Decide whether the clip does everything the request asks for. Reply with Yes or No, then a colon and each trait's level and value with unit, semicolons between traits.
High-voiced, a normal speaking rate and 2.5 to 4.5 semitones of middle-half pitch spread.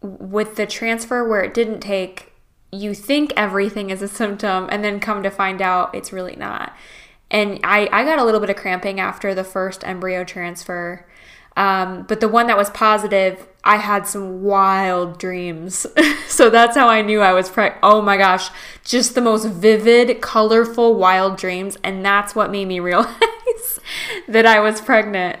Yes: high, 205 Hz; average, 180 wpm; average, 2.8 semitones